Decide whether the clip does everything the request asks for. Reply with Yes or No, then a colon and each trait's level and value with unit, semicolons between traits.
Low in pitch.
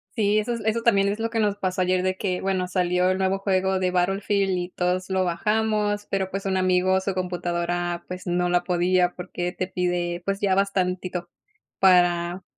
No: medium, 185 Hz